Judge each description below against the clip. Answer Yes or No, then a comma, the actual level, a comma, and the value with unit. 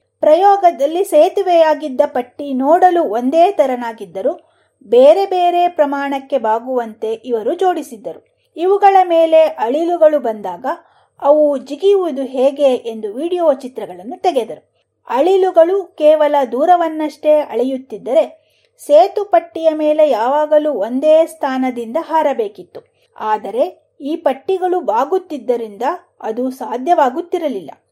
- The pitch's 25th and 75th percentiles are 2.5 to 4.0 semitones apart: No, average, 4.7 semitones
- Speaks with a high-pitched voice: Yes, very high, 305 Hz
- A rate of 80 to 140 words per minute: Yes, average, 85 wpm